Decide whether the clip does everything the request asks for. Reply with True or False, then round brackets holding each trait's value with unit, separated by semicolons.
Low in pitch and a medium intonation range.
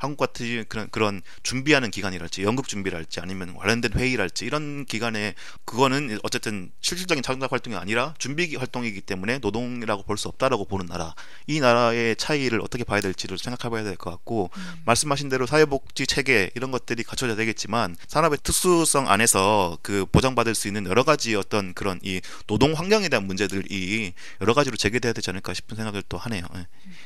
True (115 Hz; 4.7 semitones)